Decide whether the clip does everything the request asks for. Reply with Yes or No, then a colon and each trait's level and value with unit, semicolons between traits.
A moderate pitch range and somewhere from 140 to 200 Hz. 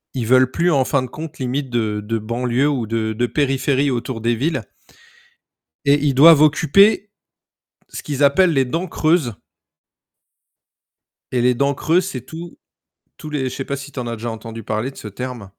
No: average, 3.8 semitones; low, 130 Hz